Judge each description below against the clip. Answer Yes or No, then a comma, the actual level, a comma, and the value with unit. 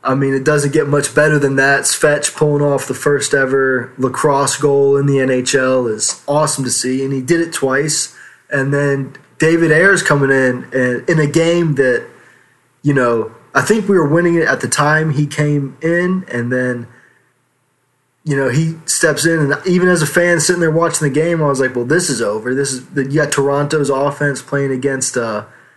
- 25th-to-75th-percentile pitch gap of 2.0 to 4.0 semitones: Yes, average, 2.7 semitones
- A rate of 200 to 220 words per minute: Yes, fast, 205 wpm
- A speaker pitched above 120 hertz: Yes, medium, 140 Hz